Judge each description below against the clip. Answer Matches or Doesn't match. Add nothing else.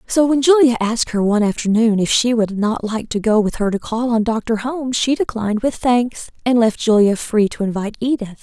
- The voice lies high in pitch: Matches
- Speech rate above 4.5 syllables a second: Matches